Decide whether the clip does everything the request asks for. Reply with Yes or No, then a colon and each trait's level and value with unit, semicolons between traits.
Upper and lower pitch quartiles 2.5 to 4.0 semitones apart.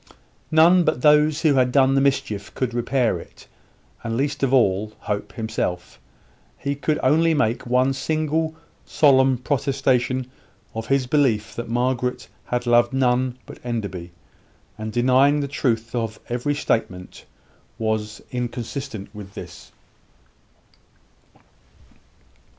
Yes: average, 3.5 semitones